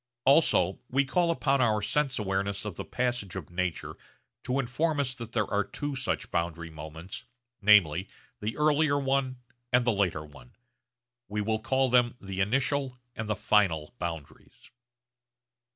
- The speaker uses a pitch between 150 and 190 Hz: No, low, 110 Hz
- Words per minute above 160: No, average, 150 wpm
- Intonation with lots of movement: Yes, wide, 5.8 semitones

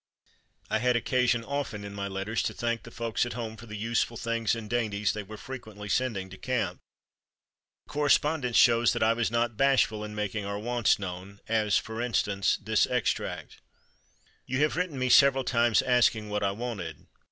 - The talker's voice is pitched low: Yes, low, 115 Hz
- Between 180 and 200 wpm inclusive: Yes, average, 185 wpm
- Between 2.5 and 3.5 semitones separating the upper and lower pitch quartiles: Yes, average, 2.9 semitones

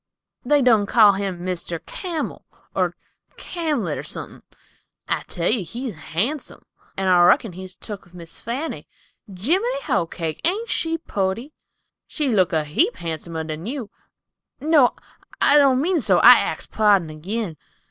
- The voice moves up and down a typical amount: No, wide, 8.8 semitones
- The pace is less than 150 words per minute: Yes, average, 140 wpm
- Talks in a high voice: Yes, high, 210 Hz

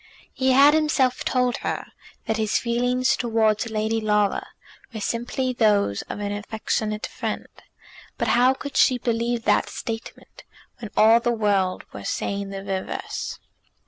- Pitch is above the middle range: Yes, high, 225 Hz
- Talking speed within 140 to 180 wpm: Yes, average, 145 wpm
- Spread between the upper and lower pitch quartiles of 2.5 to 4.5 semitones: Yes, average, 2.9 semitones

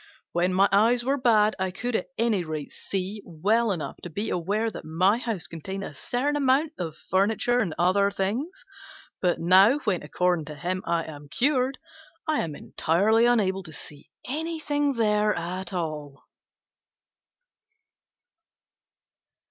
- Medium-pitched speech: No, high, 195 Hz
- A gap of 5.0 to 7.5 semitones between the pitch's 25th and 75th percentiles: Yes, wide, 5.4 semitones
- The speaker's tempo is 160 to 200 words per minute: No, average, 145 wpm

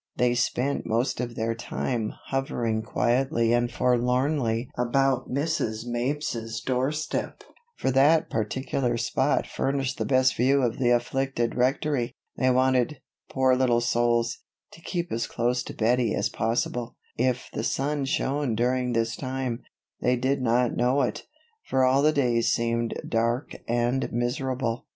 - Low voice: Yes, low, 125 Hz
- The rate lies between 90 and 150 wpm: Yes, average, 140 wpm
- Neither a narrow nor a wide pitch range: No, narrow, 2.1 semitones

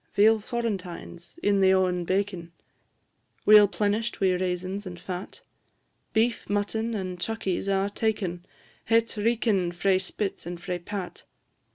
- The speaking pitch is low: No, high, 195 Hz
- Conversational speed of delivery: No, slow, 130 wpm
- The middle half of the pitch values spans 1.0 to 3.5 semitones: Yes, average, 2.9 semitones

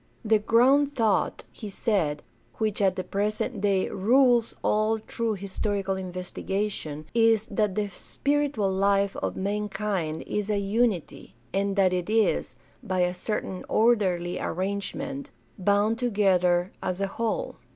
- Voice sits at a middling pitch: No, high, 205 Hz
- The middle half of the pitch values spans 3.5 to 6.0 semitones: No, average, 2.9 semitones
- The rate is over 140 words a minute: No, slow, 135 wpm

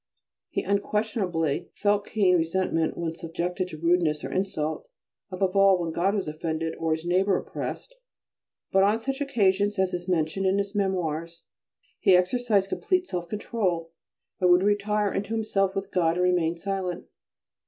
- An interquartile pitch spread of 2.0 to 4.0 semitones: Yes, average, 3.0 semitones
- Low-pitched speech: No, medium, 185 Hz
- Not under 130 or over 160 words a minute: Yes, average, 155 wpm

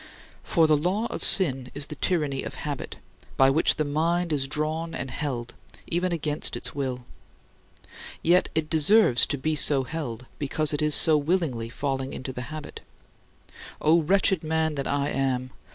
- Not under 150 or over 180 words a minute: Yes, average, 165 wpm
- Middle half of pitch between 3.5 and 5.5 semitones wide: No, average, 3.1 semitones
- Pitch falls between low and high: Yes, medium, 150 Hz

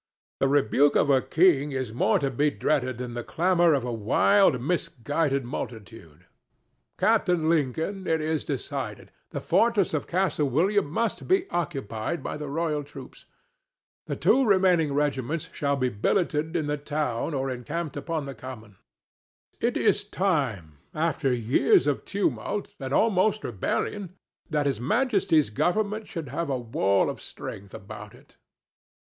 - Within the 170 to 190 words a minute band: No, average, 145 wpm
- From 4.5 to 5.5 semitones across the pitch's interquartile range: Yes, average, 5.1 semitones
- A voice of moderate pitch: Yes, medium, 145 Hz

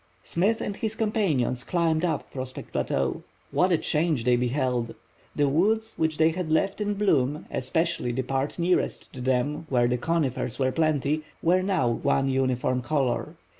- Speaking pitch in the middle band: Yes, medium, 150 Hz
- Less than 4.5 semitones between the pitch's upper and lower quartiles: No, average, 5.2 semitones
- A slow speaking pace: No, average, 165 wpm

